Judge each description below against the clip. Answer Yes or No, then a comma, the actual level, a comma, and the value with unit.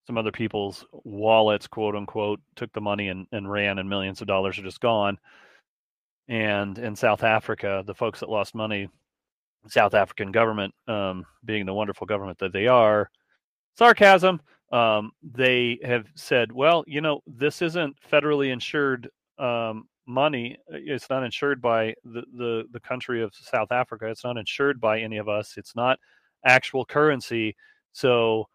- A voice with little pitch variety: No, average, 3.7 semitones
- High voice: No, low, 115 Hz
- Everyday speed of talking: Yes, average, 160 wpm